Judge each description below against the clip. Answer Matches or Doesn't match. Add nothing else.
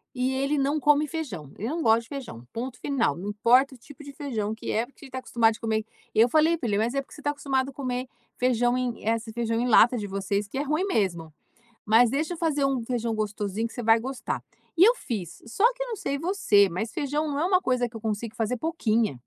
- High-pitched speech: Matches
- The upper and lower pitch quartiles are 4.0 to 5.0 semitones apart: Matches